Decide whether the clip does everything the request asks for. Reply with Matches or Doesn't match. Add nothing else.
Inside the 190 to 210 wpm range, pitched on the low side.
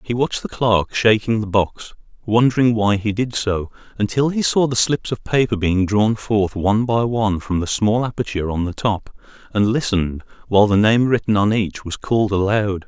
Matches